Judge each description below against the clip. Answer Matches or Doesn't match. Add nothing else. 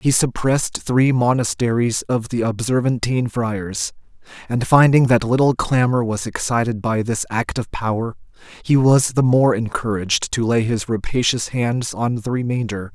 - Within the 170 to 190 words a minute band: Doesn't match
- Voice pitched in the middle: Doesn't match